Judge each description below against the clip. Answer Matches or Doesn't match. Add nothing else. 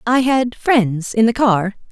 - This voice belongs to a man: Doesn't match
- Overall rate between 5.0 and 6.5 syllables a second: Doesn't match